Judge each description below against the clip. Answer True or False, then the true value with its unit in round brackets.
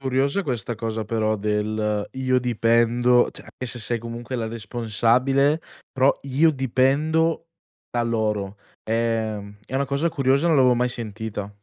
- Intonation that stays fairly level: False (3.3 semitones)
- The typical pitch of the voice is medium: False (120 Hz)